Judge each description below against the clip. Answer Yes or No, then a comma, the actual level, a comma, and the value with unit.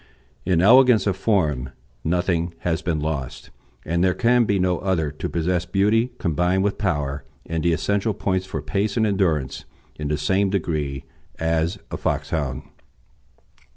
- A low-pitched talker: Yes, very low, 90 Hz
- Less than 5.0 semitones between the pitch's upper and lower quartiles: Yes, average, 4.0 semitones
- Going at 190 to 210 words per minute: No, average, 155 wpm